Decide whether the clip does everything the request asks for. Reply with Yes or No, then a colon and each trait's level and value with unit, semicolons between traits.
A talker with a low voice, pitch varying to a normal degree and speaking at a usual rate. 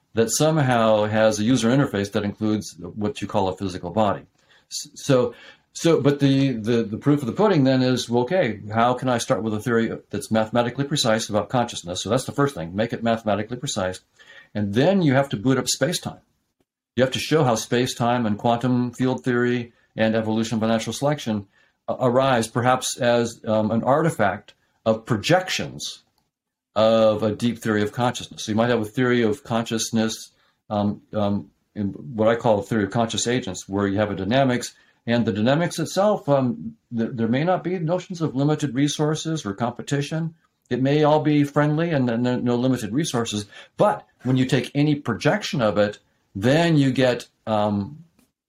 Yes: low, 120 Hz; average, 3.9 semitones; average, 185 wpm